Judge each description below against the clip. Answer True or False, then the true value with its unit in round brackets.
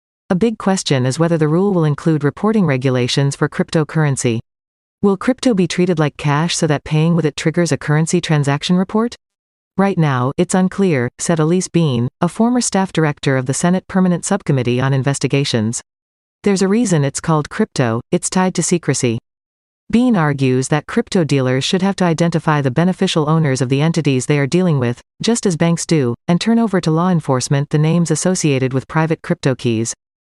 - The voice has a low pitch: False (160 Hz)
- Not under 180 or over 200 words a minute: True (185 wpm)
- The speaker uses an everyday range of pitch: True (4.8 semitones)